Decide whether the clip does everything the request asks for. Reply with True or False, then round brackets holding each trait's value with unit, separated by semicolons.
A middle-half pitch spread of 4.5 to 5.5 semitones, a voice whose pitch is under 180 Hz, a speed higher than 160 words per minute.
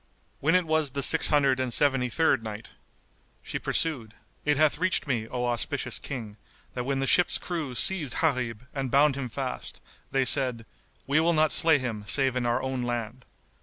False (3.6 semitones; 135 Hz; 185 wpm)